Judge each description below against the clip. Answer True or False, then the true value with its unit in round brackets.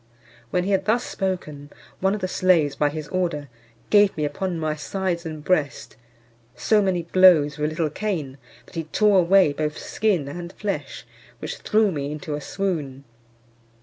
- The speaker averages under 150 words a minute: False (175 wpm)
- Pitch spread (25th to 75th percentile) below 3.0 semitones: False (4.3 semitones)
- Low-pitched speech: False (170 Hz)